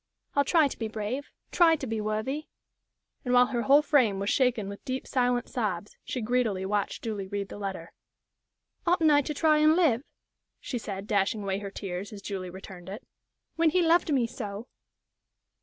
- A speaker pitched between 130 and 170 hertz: No, high, 225 Hz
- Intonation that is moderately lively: No, wide, 5.9 semitones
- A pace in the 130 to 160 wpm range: No, average, 190 wpm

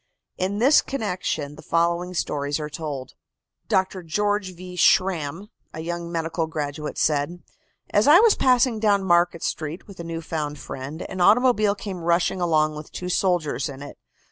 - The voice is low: No, medium, 170 Hz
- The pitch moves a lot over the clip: No, average, 4.0 semitones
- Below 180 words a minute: Yes, average, 165 wpm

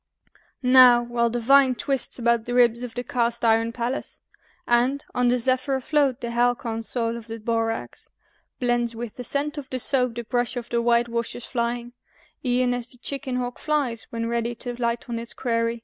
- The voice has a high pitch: Yes, high, 240 Hz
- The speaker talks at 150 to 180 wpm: No, average, 195 wpm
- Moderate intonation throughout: No, narrow, 1.3 semitones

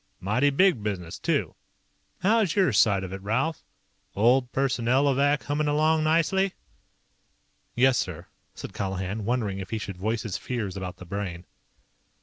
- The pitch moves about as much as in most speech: No, wide, 6.7 semitones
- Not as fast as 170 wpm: Yes, average, 140 wpm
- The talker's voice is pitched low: Yes, low, 120 Hz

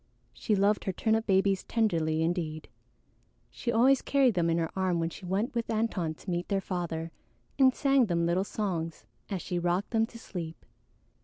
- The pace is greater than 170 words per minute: Yes, average, 180 wpm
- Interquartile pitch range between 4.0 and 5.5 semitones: Yes, average, 4.8 semitones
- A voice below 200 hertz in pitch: Yes, high, 190 Hz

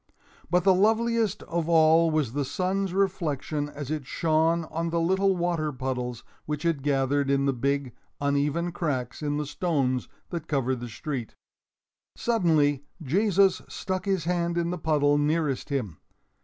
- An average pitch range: Yes, average, 3.8 semitones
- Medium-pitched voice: Yes, medium, 155 Hz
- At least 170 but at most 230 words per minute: No, average, 155 wpm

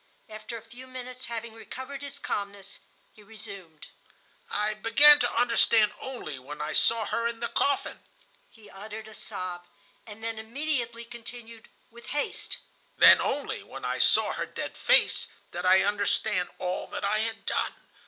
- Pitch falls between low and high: No, high, 225 Hz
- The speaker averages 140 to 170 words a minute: Yes, average, 160 wpm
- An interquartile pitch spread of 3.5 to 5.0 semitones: No, average, 2.7 semitones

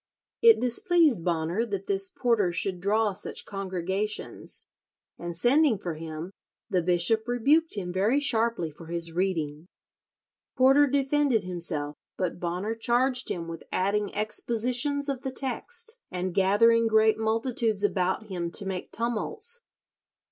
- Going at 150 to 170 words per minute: No, slow, 135 wpm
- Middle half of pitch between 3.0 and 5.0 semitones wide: No, wide, 5.4 semitones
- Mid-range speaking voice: No, high, 210 Hz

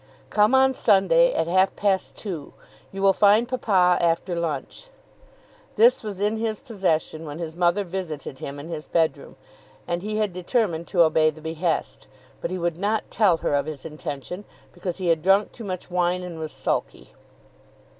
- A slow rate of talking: No, average, 175 wpm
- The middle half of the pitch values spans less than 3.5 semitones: No, average, 4.2 semitones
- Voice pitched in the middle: Yes, medium, 180 Hz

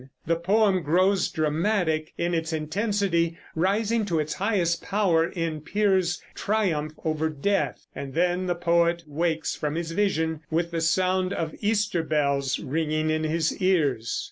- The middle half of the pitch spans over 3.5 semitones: No, average, 3.2 semitones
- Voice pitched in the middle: Yes, medium, 170 Hz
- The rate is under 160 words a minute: Yes, average, 145 wpm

